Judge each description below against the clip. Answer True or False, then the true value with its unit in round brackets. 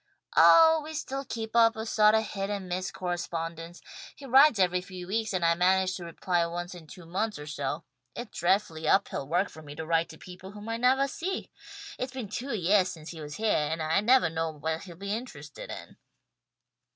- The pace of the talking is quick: True (210 wpm)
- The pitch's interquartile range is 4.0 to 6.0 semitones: True (5.0 semitones)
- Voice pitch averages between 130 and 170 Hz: False (185 Hz)